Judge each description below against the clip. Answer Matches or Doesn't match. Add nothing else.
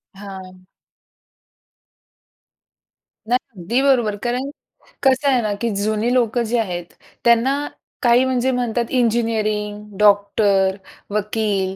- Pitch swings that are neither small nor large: Matches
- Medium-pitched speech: Doesn't match